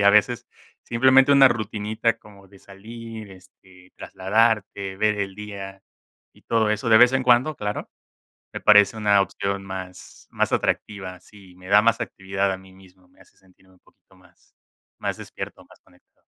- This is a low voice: Yes, low, 100 Hz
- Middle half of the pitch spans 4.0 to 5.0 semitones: No, average, 2.8 semitones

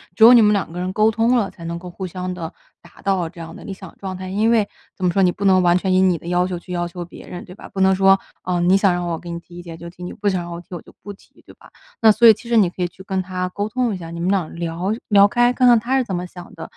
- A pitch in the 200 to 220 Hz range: No, medium, 185 Hz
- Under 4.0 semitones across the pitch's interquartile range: Yes, narrow, 2.6 semitones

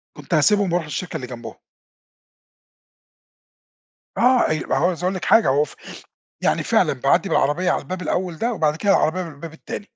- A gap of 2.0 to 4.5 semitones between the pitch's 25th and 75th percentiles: Yes, average, 3.4 semitones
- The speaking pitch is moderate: Yes, medium, 175 Hz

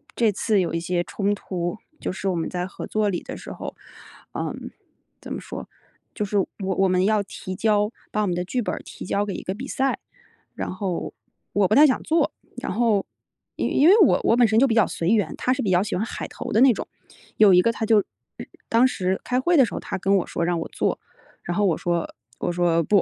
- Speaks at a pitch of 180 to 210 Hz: Yes, high, 200 Hz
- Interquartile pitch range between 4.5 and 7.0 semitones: No, average, 3.9 semitones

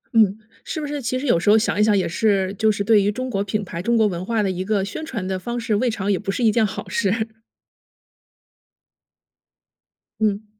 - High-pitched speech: Yes, high, 210 Hz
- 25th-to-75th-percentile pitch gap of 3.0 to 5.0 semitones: No, narrow, 2.6 semitones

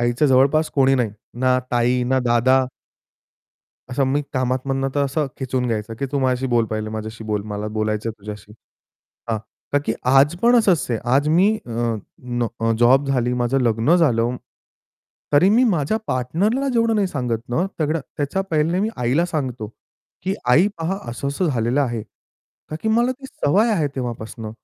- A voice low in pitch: Yes, low, 130 Hz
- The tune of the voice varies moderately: Yes, average, 4.9 semitones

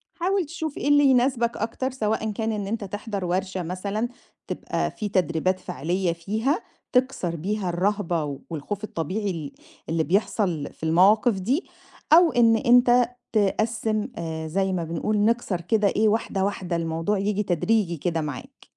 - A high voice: Yes, high, 205 Hz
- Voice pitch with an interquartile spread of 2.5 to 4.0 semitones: No, average, 4.6 semitones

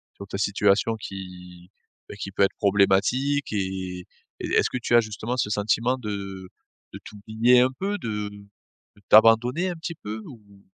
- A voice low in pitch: Yes, low, 105 Hz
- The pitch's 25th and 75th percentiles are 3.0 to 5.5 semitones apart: Yes, average, 3.5 semitones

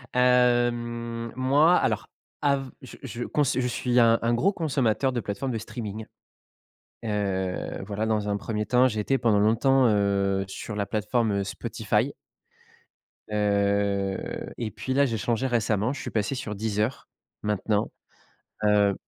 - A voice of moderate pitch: No, low, 110 Hz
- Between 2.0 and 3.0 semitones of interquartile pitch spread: No, average, 3.4 semitones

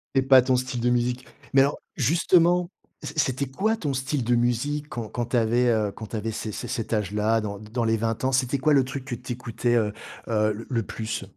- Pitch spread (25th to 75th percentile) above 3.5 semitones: No, average, 3.0 semitones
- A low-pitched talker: Yes, low, 120 Hz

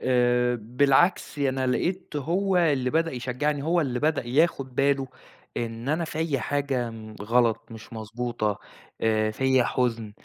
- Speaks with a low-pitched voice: Yes, low, 130 Hz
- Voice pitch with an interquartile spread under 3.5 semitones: No, average, 3.8 semitones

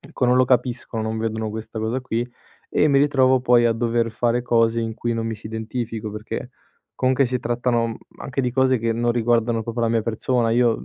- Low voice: Yes, low, 115 Hz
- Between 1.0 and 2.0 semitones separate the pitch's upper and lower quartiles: Yes, narrow, 1.7 semitones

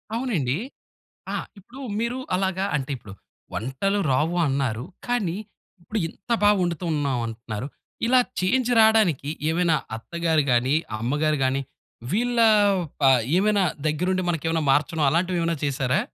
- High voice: No, medium, 165 Hz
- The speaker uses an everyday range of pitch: No, wide, 6.3 semitones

